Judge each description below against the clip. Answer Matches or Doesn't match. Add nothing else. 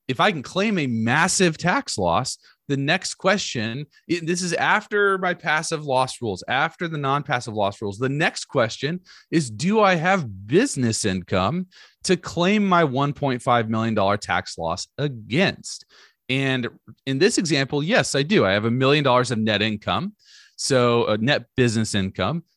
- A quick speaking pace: Doesn't match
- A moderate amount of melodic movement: Doesn't match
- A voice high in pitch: Doesn't match